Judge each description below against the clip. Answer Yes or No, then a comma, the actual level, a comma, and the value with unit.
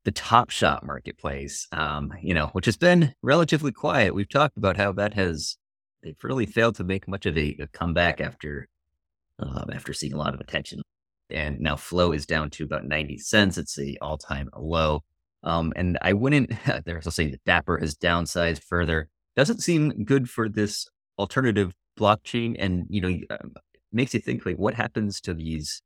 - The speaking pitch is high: No, very low, 85 Hz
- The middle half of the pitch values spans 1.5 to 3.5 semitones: No, wide, 5.4 semitones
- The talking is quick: No, average, 185 wpm